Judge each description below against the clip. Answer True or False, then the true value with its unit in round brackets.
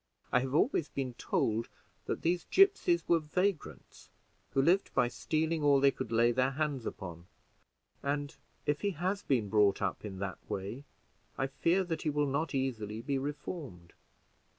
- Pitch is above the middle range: False (140 Hz)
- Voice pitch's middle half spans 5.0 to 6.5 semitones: True (5.6 semitones)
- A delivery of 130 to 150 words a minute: False (165 wpm)